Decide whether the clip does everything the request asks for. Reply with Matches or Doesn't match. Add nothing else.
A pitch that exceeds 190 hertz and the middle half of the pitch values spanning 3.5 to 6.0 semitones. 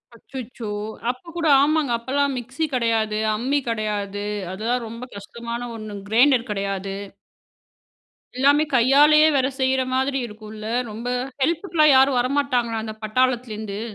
Matches